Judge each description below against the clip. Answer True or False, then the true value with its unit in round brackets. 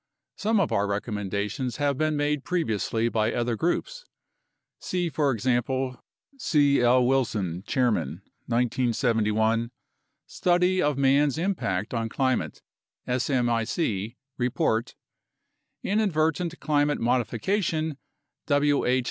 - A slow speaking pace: True (100 wpm)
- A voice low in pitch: True (130 Hz)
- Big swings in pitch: False (4.9 semitones)